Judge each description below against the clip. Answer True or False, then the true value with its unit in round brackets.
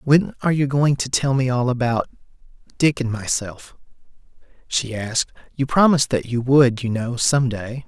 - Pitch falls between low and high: False (130 Hz)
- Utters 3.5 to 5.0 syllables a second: True (4.9 syllables/s)